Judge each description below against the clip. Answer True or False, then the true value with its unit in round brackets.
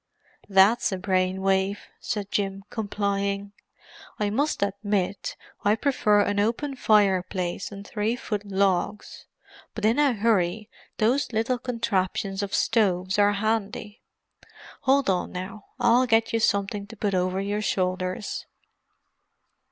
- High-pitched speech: True (205 Hz)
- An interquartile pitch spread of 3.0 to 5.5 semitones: False (2.5 semitones)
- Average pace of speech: False (120 wpm)